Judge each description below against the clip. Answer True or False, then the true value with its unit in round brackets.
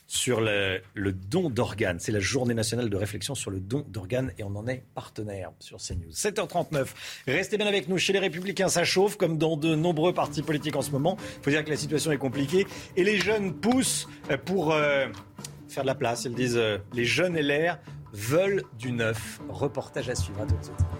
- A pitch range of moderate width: False (7.1 semitones)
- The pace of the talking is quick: False (210 wpm)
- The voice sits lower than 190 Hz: True (140 Hz)